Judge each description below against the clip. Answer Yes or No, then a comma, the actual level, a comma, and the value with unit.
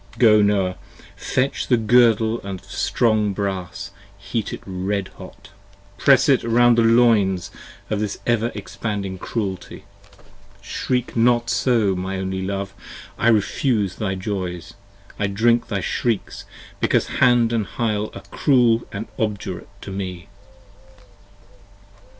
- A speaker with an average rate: No, slow, 130 wpm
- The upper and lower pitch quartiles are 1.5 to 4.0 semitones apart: Yes, average, 3.3 semitones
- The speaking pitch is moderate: No, low, 105 Hz